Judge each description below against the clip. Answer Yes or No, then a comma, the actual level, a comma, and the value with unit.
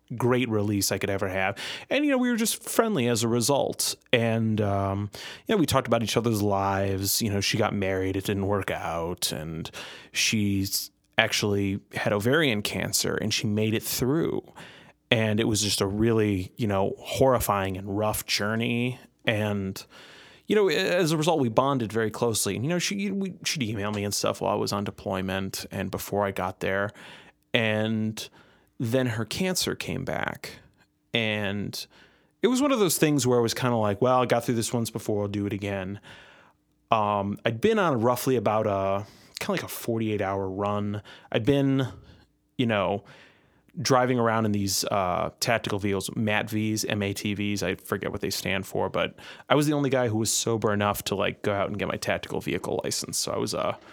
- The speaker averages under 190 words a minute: No, average, 195 wpm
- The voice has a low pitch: Yes, low, 110 Hz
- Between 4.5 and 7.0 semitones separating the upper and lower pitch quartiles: No, average, 3.6 semitones